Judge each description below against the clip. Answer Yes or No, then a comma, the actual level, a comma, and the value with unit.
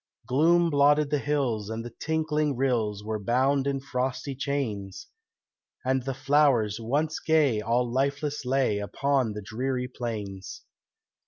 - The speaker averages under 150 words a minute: Yes, slow, 135 wpm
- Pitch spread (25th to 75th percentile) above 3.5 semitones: Yes, average, 4.0 semitones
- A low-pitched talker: Yes, low, 130 Hz